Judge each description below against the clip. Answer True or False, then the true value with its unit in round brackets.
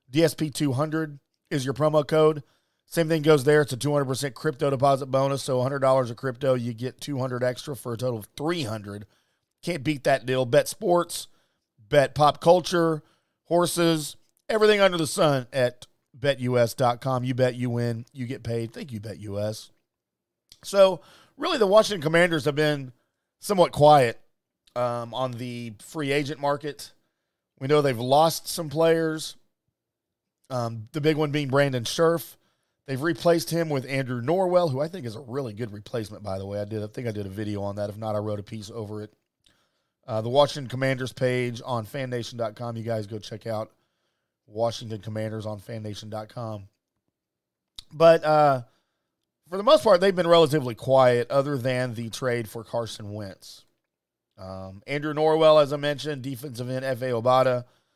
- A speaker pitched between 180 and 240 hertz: False (130 Hz)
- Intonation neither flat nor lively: True (4.8 semitones)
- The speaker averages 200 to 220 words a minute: False (165 wpm)